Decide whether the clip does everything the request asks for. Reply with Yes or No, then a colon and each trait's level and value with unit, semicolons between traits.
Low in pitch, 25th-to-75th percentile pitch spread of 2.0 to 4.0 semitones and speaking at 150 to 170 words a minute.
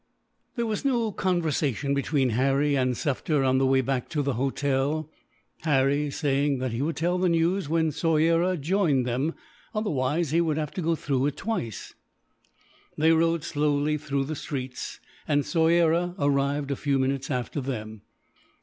No: medium, 145 Hz; average, 3.5 semitones; average, 160 wpm